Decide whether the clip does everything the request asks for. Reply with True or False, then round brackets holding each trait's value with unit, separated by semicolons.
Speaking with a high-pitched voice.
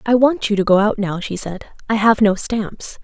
True (210 Hz)